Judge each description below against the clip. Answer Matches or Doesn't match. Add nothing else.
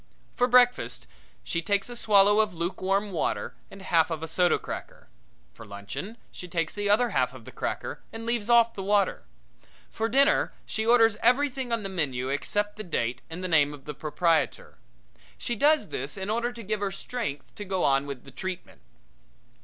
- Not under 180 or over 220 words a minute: Matches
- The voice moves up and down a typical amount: Doesn't match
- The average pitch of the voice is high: Matches